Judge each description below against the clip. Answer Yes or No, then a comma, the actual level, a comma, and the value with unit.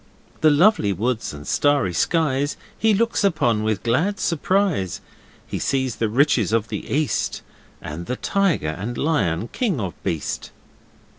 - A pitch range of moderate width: No, wide, 7.8 semitones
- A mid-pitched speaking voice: No, low, 130 Hz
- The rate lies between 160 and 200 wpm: No, average, 145 wpm